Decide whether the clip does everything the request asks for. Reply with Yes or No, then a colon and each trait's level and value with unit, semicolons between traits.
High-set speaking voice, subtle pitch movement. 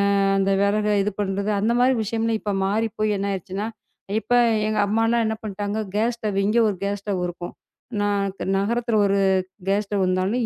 Yes: high, 210 Hz; narrow, 2.0 semitones